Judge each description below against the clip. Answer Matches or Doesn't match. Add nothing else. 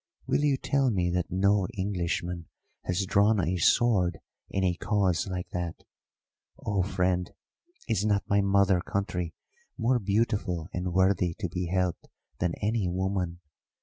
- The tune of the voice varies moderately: Doesn't match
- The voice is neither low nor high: Doesn't match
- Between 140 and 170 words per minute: Matches